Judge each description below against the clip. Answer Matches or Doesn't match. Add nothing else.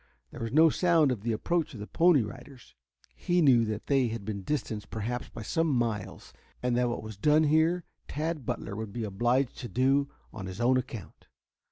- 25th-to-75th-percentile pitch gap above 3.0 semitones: Matches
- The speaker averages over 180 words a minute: Matches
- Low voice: Matches